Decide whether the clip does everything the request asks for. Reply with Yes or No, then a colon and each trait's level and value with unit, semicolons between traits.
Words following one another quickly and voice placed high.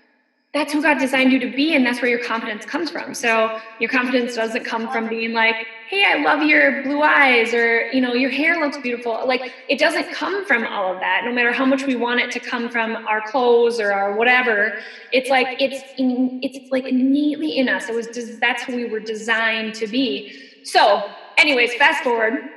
Yes: fast, 215 wpm; very high, 250 Hz